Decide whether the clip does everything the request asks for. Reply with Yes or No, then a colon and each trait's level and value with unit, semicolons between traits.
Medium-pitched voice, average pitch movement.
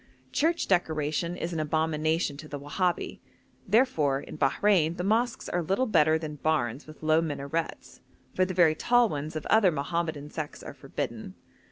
Yes: medium, 160 Hz; average, 3.3 semitones